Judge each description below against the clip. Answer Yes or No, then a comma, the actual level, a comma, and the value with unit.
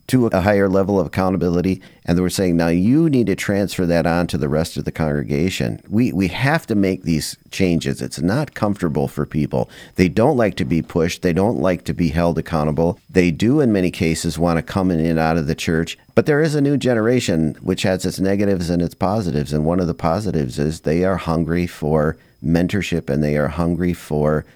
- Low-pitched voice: Yes, very low, 85 Hz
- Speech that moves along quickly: Yes, fast, 220 wpm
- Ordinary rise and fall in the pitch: Yes, average, 3.0 semitones